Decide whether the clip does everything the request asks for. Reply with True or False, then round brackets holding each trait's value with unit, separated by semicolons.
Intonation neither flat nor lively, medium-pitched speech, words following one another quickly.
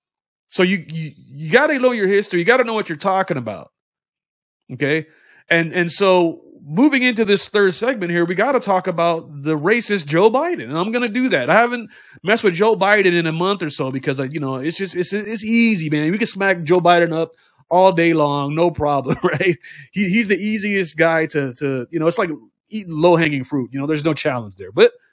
True (5.0 semitones; 175 Hz; 220 wpm)